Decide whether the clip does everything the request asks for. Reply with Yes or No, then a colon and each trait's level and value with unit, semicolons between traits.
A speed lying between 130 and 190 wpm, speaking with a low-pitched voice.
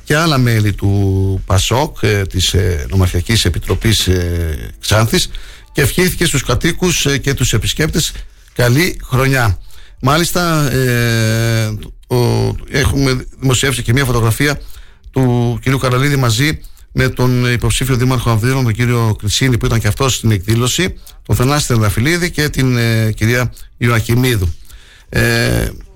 Yes: average, 145 wpm; low, 120 Hz